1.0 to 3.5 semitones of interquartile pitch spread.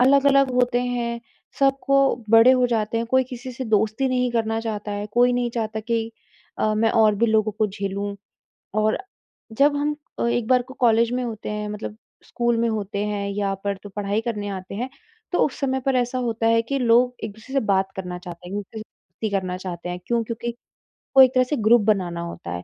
Yes: average, 3.1 semitones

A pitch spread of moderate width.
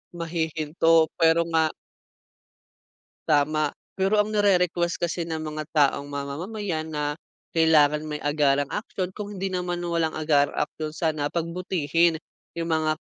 No: narrow, 2.3 semitones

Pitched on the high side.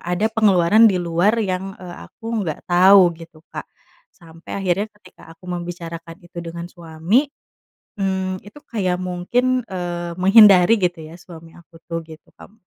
No: medium, 180 Hz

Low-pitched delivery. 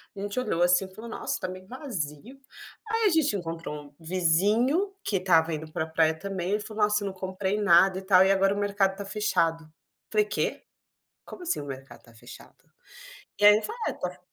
No: high, 190 Hz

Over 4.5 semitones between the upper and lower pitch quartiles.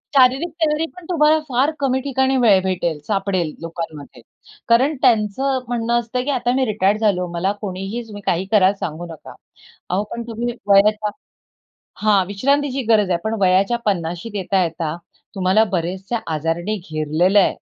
Yes: average, 5.1 semitones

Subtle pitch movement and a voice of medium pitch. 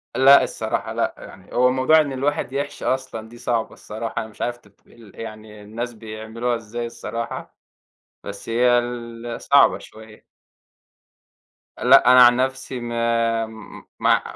No: narrow, 2.2 semitones; low, 120 Hz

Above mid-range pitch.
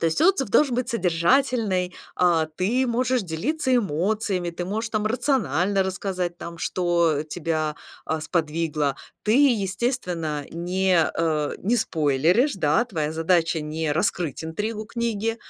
No: medium, 180 Hz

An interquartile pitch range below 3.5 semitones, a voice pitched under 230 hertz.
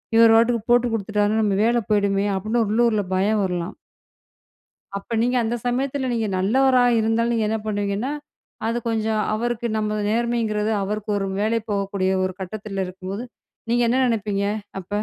Yes: average, 2.7 semitones; high, 215 Hz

